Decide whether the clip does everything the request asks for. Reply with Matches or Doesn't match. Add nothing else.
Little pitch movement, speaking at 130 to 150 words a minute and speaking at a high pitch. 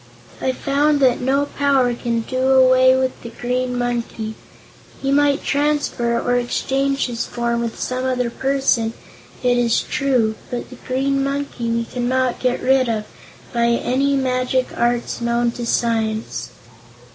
Matches